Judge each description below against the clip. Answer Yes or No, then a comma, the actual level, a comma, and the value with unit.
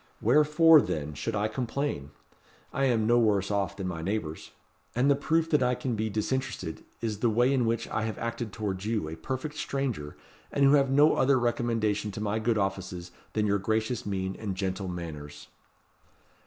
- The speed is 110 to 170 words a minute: No, average, 185 wpm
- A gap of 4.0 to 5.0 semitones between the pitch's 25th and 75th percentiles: Yes, average, 4.7 semitones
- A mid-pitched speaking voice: No, low, 110 Hz